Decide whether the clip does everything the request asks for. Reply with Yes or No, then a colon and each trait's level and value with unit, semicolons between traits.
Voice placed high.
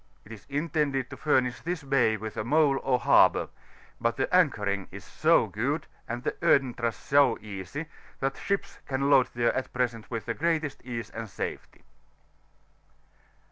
No: low, 130 Hz